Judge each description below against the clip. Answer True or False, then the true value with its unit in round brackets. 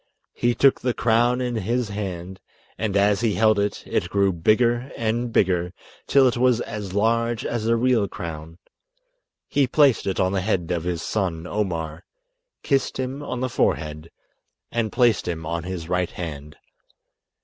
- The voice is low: True (105 Hz)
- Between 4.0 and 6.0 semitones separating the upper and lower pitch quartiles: True (5.2 semitones)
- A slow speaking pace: False (165 wpm)